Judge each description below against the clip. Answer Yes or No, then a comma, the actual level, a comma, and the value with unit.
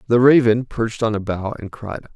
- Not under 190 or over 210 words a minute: No, fast, 225 wpm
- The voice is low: Yes, low, 110 Hz